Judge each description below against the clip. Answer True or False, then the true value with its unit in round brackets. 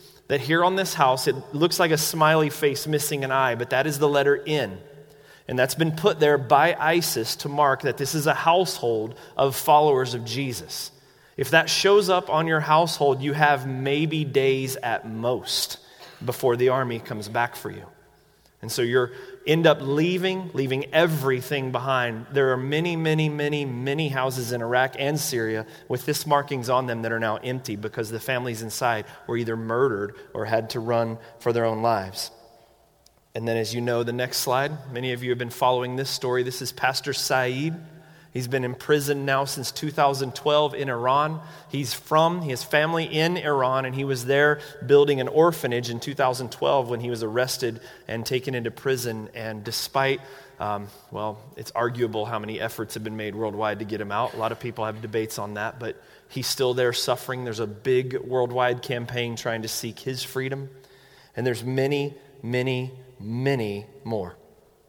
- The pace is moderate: True (185 wpm)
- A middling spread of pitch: True (3.6 semitones)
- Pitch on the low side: True (130 Hz)